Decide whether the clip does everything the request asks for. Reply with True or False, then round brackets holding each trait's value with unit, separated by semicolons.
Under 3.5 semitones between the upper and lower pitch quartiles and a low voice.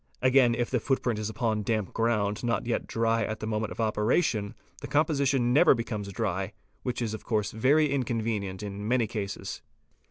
True (2.8 semitones; 115 Hz)